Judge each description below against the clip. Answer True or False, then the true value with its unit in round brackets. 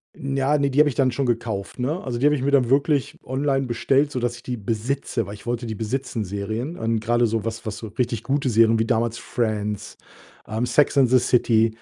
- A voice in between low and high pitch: False (120 Hz)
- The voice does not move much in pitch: False (3.3 semitones)